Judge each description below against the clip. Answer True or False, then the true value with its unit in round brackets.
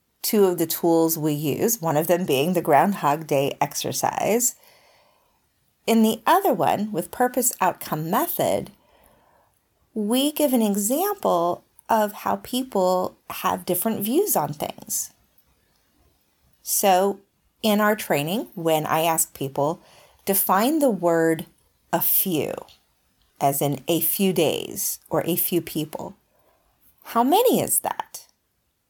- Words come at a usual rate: False (125 wpm)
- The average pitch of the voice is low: False (185 Hz)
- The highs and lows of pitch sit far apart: True (5.7 semitones)